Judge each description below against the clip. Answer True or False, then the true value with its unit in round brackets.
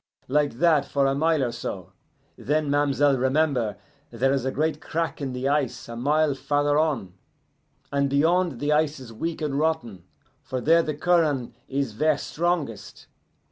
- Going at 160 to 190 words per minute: True (165 wpm)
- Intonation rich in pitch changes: False (3.1 semitones)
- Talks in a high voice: False (145 Hz)